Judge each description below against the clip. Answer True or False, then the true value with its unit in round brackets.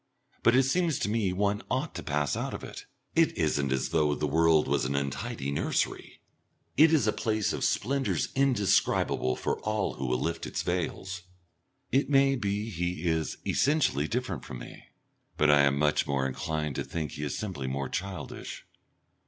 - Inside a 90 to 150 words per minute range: False (180 wpm)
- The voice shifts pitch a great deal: True (7.3 semitones)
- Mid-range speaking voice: False (85 Hz)